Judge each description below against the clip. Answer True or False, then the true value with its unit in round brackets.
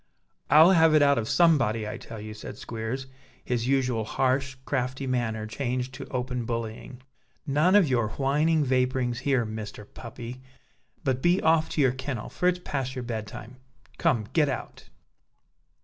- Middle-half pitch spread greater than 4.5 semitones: False (3.4 semitones)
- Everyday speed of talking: True (165 wpm)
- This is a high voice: False (130 Hz)